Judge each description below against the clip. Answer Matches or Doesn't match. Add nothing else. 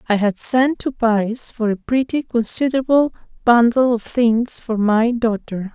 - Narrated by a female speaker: Matches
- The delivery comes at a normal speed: Matches